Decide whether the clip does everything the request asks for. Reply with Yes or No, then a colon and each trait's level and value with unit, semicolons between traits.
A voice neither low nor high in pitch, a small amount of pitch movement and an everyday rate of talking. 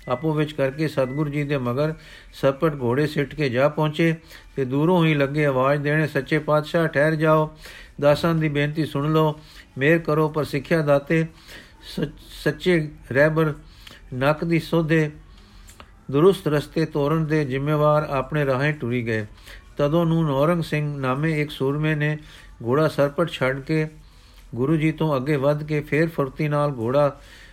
Yes: medium, 150 Hz; narrow, 2.0 semitones; average, 150 wpm